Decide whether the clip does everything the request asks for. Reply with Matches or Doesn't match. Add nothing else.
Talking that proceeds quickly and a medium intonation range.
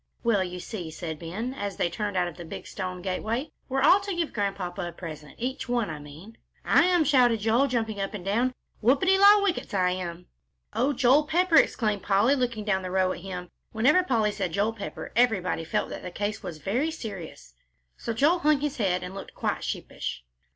Doesn't match